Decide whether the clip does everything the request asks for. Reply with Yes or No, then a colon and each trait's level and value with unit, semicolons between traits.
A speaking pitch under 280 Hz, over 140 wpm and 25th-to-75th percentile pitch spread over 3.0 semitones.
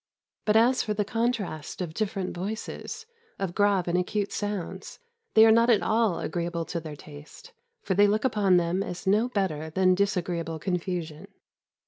Yes: high, 190 Hz; average, 165 wpm; average, 3.8 semitones